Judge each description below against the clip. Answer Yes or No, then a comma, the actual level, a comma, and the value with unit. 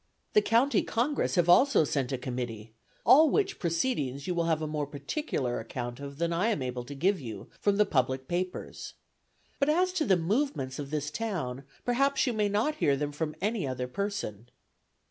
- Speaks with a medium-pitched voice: Yes, medium, 165 Hz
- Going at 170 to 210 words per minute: Yes, average, 190 wpm